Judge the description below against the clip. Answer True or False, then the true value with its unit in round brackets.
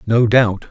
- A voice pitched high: False (110 Hz)